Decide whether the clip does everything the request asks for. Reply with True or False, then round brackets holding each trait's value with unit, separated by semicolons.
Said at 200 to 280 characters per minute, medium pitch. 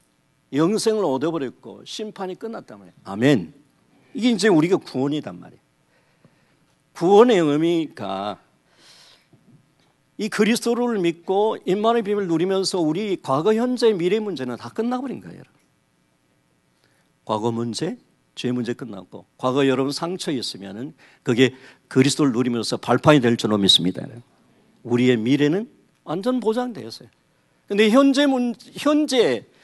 False (295 characters per minute; 165 Hz)